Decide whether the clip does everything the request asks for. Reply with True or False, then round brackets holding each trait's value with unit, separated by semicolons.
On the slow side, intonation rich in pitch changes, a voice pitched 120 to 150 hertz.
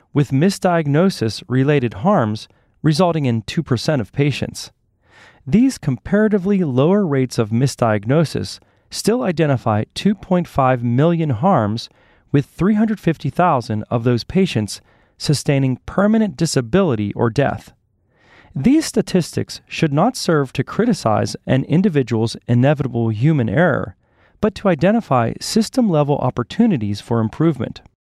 True (105 wpm; 7.5 semitones; 140 Hz)